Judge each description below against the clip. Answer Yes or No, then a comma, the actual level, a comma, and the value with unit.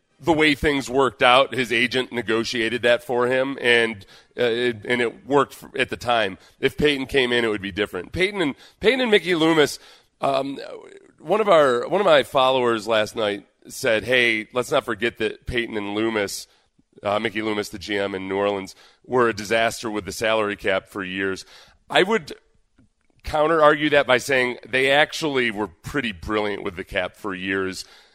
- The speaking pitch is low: Yes, low, 120 Hz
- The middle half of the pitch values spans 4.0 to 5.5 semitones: Yes, average, 4.3 semitones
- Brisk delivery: No, average, 190 wpm